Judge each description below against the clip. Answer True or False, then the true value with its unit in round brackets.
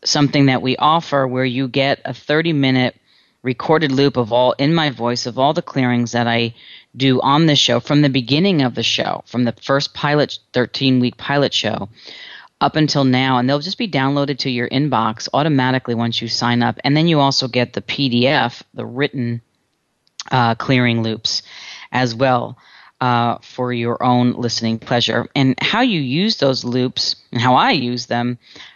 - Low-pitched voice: True (130 Hz)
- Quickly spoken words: False (185 wpm)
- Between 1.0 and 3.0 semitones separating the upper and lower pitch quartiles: True (2.6 semitones)